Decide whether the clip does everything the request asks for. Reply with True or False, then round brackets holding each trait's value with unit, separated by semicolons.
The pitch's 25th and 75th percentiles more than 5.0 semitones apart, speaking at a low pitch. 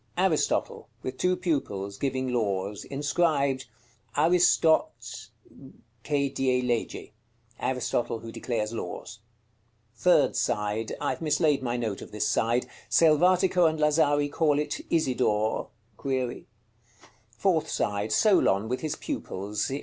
True (5.4 semitones; 130 Hz)